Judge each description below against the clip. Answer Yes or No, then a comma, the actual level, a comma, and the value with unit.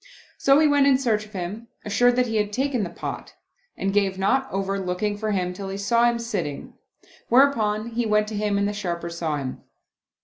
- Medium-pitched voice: No, high, 210 Hz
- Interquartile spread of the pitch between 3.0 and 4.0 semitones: Yes, average, 3.5 semitones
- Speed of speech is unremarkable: No, fast, 210 wpm